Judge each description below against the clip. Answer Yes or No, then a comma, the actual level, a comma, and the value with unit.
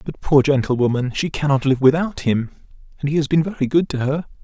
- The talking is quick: Yes, fast, 215 wpm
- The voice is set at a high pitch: No, medium, 140 Hz